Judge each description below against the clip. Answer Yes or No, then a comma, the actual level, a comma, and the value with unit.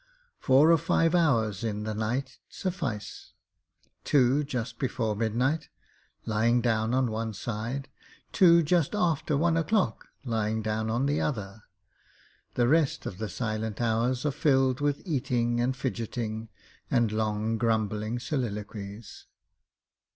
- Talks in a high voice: No, low, 120 Hz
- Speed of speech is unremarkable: No, slow, 130 wpm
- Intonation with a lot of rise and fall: No, average, 4.2 semitones